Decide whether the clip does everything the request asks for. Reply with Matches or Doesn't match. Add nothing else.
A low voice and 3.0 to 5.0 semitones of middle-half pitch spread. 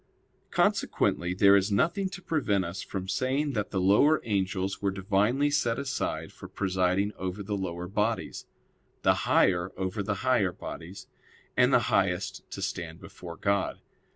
Matches